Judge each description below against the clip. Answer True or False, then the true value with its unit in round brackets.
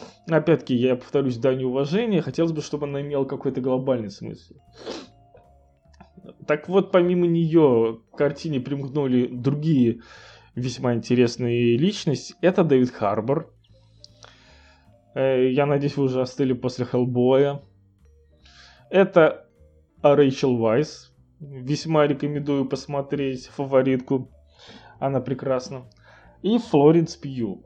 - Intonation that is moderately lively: True (3.6 semitones)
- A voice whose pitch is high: False (130 Hz)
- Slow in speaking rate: True (100 wpm)